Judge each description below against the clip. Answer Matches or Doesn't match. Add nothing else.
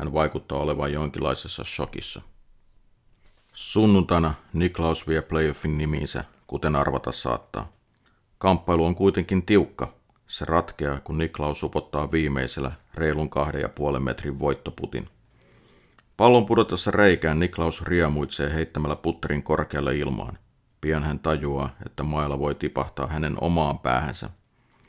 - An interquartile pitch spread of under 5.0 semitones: Matches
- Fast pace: Doesn't match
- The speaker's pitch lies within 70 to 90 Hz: Matches